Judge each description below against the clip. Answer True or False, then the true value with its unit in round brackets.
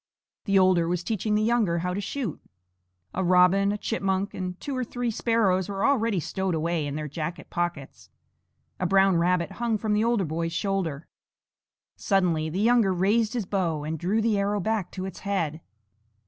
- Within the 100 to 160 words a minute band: False (180 wpm)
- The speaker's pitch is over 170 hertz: True (190 Hz)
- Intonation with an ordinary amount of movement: True (3.6 semitones)